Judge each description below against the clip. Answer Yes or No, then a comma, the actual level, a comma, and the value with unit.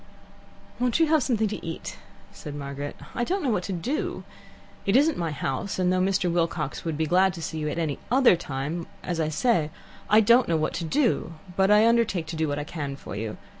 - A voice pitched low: No, medium, 175 Hz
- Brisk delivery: Yes, fast, 230 wpm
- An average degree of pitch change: No, wide, 6.2 semitones